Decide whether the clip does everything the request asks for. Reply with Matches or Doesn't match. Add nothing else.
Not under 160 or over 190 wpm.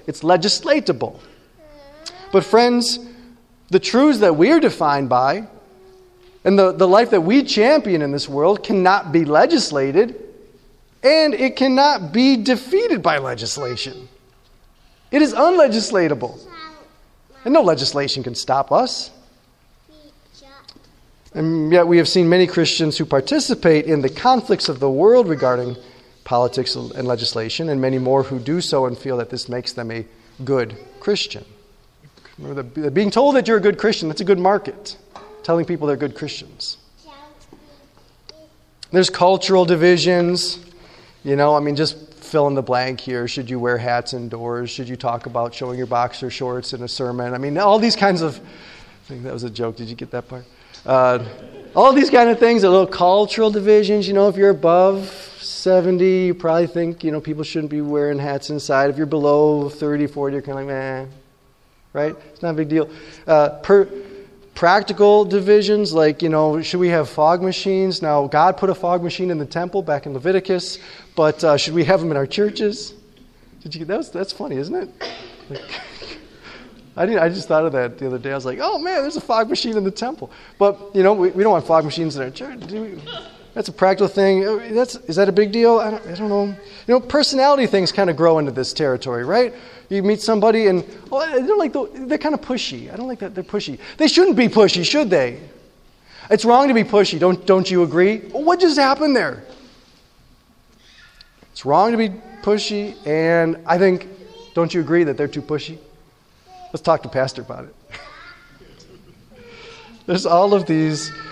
Matches